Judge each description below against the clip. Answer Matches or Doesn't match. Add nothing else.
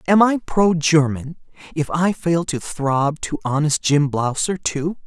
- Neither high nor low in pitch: Matches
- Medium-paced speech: Matches